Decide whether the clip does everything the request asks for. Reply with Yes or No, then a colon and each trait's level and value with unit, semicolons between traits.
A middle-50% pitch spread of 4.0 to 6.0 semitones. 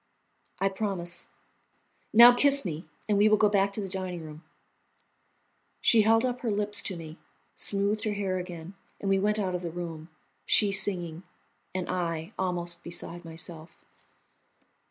No: average, 3.3 semitones